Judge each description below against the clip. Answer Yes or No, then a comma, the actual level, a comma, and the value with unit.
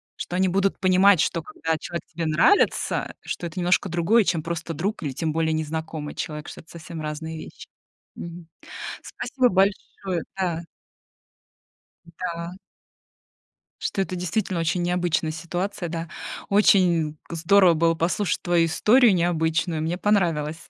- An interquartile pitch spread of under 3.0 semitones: Yes, narrow, 2.4 semitones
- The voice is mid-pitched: Yes, medium, 170 Hz